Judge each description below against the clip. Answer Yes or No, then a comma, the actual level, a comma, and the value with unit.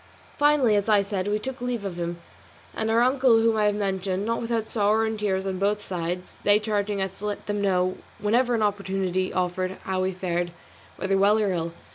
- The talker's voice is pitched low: No, high, 205 Hz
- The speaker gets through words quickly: Yes, fast, 215 wpm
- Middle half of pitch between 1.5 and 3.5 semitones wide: Yes, average, 2.7 semitones